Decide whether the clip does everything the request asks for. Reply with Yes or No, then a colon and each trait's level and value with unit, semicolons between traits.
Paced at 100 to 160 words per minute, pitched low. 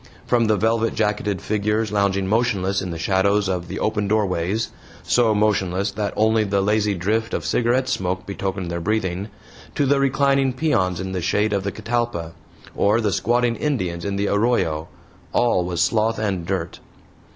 No: average, 170 wpm; low, 105 Hz